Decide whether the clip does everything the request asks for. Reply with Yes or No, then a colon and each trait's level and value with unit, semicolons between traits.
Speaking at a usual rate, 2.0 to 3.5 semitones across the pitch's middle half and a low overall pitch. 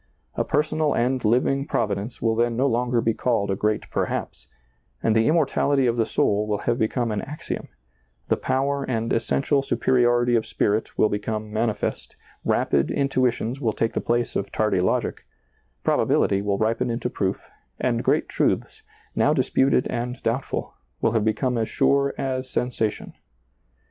Yes: average, 170 wpm; average, 3.1 semitones; low, 120 Hz